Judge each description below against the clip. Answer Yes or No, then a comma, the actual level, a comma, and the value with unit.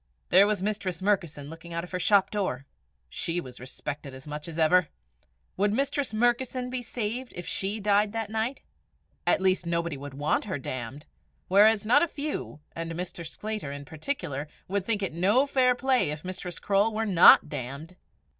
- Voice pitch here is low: No, medium, 185 Hz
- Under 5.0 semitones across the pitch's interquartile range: No, wide, 5.6 semitones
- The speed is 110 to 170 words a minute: No, average, 180 wpm